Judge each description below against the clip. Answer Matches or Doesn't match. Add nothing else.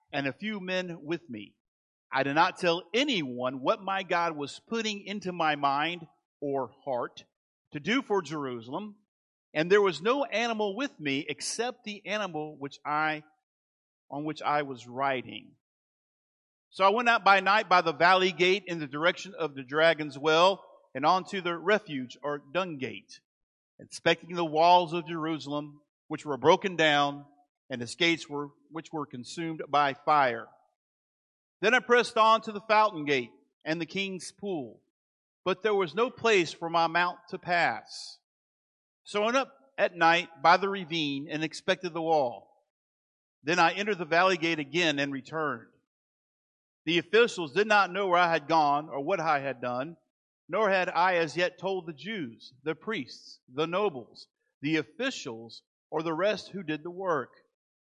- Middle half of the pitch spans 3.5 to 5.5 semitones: Matches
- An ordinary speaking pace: Matches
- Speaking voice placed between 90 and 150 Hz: Doesn't match